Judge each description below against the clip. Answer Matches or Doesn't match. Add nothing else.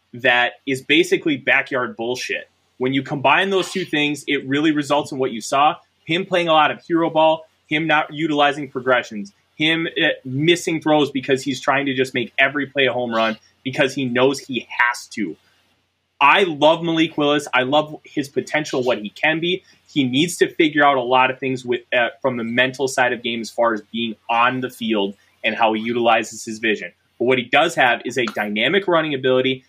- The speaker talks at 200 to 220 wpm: Matches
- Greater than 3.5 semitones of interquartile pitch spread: Matches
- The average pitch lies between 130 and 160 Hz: Matches